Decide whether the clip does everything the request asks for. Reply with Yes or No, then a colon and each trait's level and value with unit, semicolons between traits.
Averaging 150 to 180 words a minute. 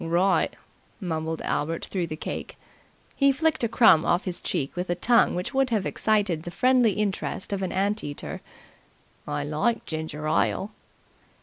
Yes: average, 165 wpm